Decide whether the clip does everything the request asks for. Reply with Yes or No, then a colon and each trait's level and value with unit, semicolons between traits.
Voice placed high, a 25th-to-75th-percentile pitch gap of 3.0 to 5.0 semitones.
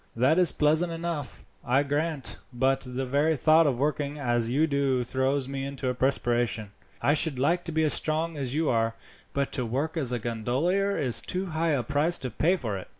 No: medium, 140 Hz; average, 4.0 semitones